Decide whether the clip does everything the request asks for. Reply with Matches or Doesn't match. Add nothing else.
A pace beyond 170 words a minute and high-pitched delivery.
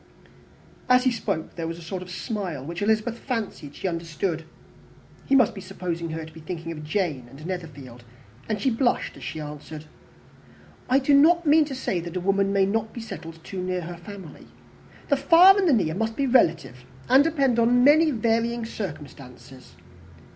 Matches